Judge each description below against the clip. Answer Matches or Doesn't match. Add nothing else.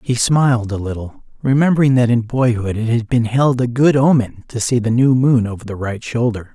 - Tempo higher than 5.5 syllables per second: Doesn't match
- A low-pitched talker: Matches